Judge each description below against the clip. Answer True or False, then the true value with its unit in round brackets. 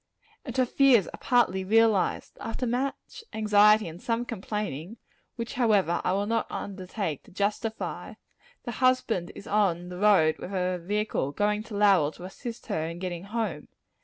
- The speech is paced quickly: False (160 wpm)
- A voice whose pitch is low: False (210 Hz)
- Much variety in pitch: False (3.8 semitones)